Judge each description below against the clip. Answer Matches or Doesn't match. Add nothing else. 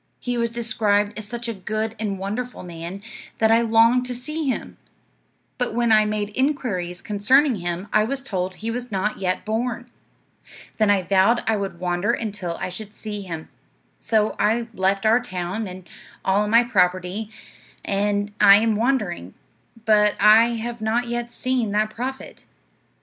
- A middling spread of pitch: Matches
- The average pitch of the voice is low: Doesn't match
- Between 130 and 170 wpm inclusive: Matches